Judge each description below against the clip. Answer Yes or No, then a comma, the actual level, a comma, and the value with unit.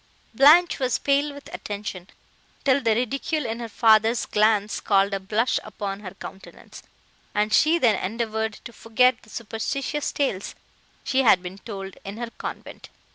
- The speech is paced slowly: No, average, 155 wpm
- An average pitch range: Yes, average, 4.1 semitones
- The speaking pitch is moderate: No, high, 225 Hz